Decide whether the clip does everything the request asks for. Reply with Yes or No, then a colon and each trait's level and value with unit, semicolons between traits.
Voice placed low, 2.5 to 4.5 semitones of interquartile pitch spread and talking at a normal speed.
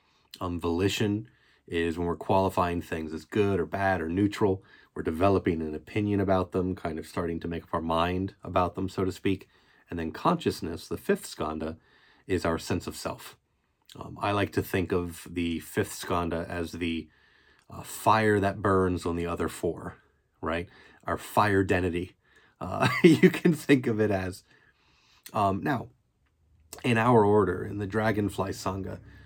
Yes: very low, 95 Hz; average, 3.2 semitones; average, 170 wpm